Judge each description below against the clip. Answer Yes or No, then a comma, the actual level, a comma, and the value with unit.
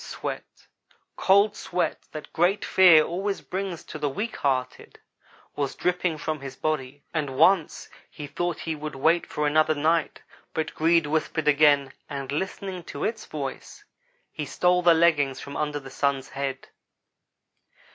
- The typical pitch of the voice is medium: Yes, medium, 155 Hz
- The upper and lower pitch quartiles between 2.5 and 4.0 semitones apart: Yes, average, 3.4 semitones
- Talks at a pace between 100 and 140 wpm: No, average, 155 wpm